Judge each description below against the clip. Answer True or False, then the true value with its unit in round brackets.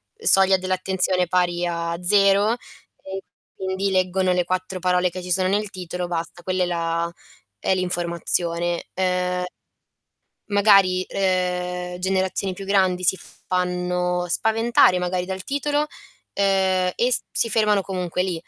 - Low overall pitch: False (185 Hz)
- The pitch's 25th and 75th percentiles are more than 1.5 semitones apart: False (1.2 semitones)